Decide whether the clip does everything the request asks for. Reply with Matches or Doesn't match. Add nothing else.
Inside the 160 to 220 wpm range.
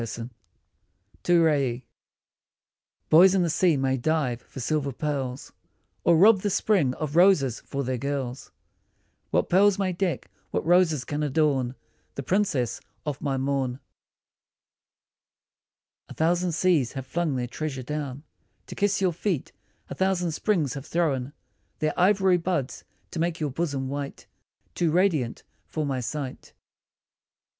Doesn't match